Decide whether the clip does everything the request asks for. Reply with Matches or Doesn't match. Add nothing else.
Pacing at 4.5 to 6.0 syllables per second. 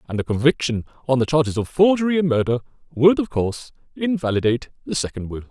Doesn't match